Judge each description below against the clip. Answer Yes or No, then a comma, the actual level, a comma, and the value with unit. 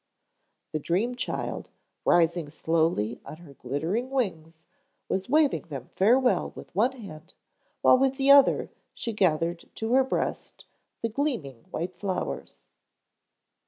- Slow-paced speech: Yes, slow, 125 wpm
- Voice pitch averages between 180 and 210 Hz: Yes, medium, 185 Hz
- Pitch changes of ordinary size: No, wide, 7.7 semitones